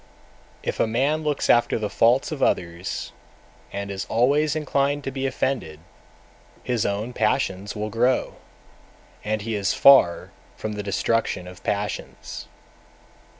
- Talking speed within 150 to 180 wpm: No, average, 140 wpm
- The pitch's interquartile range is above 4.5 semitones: Yes, average, 5.0 semitones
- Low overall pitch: Yes, low, 115 Hz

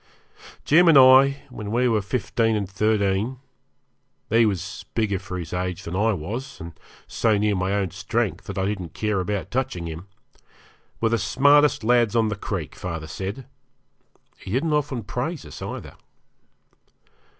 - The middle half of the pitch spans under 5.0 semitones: Yes, average, 4.4 semitones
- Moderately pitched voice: No, low, 105 Hz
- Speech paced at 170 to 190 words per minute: No, average, 160 wpm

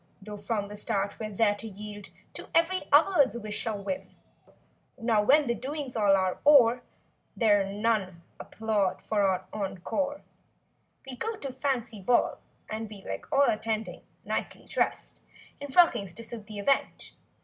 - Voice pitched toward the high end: Yes, high, 220 Hz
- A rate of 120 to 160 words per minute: Yes, average, 150 wpm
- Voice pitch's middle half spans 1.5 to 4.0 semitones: No, average, 4.5 semitones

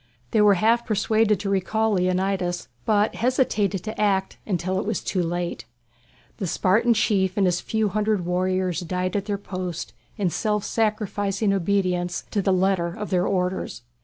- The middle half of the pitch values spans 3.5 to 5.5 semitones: No, narrow, 2.6 semitones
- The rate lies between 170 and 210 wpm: No, average, 160 wpm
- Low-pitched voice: No, high, 195 Hz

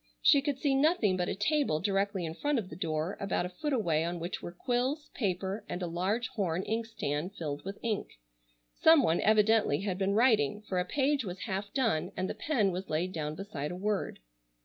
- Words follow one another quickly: Yes, fast, 210 wpm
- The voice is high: Yes, high, 195 Hz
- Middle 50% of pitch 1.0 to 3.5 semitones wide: No, average, 4.7 semitones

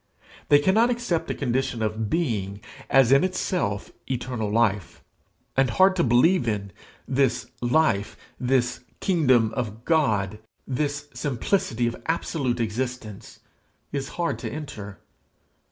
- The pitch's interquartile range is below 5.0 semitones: No, wide, 5.4 semitones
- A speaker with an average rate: No, slow, 120 wpm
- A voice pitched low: Yes, low, 125 Hz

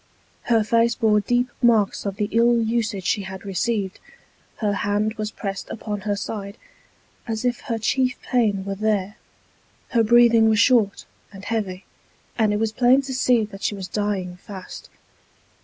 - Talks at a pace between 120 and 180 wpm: Yes, average, 165 wpm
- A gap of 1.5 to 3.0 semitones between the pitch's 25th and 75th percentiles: Yes, narrow, 2.6 semitones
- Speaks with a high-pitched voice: Yes, high, 215 Hz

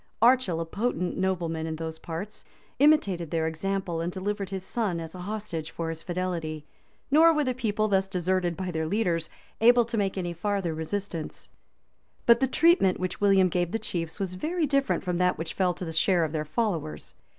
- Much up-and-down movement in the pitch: No, average, 4.1 semitones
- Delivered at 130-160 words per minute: No, average, 195 wpm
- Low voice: No, medium, 185 Hz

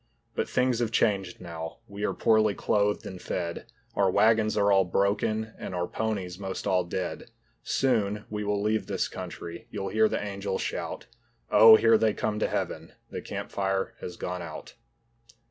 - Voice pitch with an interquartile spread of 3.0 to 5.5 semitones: No, narrow, 2.6 semitones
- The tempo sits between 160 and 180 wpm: Yes, average, 170 wpm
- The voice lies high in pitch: No, low, 100 Hz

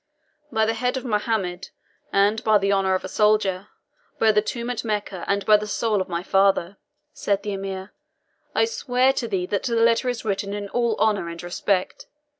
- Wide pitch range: No, narrow, 2.6 semitones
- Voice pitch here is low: No, high, 205 Hz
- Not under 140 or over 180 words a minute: No, average, 200 wpm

